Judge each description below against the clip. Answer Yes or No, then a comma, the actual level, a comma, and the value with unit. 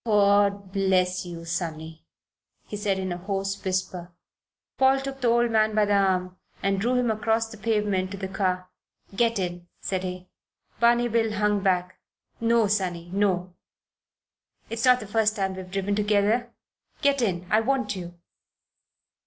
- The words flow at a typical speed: Yes, average, 160 wpm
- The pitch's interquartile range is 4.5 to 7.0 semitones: No, average, 3.3 semitones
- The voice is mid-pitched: No, high, 200 Hz